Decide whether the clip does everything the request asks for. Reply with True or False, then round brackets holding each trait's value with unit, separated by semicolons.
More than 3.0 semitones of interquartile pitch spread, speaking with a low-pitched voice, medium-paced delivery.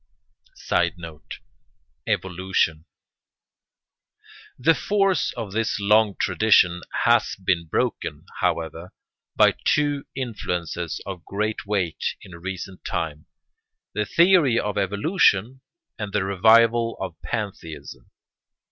False (4.7 semitones; 100 Hz; 100 wpm)